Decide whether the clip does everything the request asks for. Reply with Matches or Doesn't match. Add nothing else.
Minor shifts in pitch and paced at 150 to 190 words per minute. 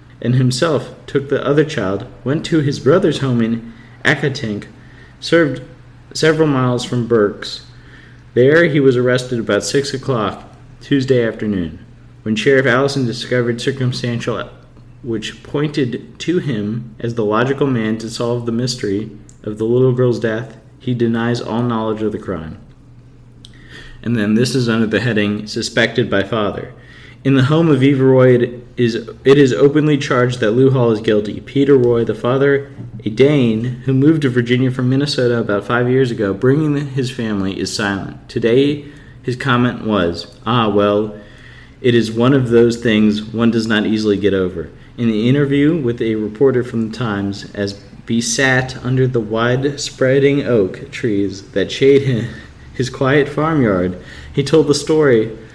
Doesn't match